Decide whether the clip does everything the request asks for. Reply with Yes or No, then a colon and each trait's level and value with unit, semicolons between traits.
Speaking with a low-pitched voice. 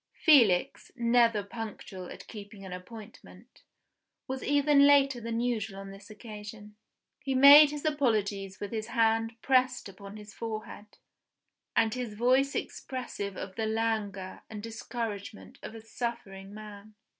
No: high, 220 Hz